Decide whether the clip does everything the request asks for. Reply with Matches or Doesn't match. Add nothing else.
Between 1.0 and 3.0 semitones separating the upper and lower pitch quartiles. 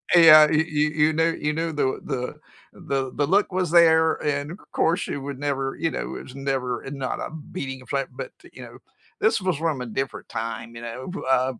Doesn't match